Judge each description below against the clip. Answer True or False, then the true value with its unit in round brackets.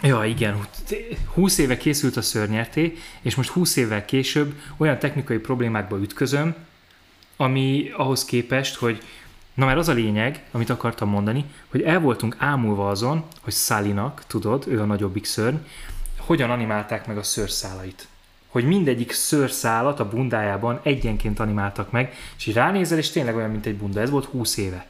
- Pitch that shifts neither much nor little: True (5.0 semitones)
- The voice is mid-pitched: False (120 Hz)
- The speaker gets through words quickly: True (160 wpm)